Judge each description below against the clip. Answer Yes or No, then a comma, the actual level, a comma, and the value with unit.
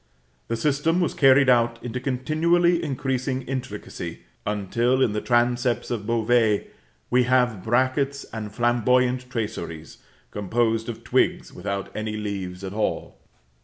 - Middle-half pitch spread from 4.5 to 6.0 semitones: No, average, 3.2 semitones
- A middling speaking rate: No, slow, 130 wpm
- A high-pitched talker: No, low, 120 Hz